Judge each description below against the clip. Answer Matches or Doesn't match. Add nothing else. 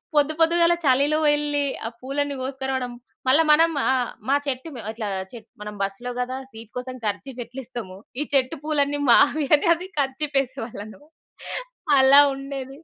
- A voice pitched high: Matches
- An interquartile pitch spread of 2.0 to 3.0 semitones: Matches